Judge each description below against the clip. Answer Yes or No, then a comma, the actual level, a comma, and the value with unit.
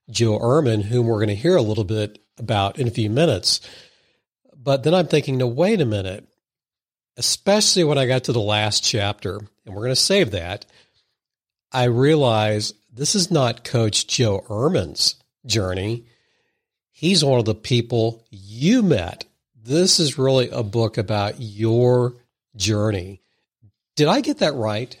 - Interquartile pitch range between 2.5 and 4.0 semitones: No, average, 5.2 semitones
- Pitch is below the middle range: Yes, low, 120 Hz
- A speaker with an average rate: Yes, average, 160 wpm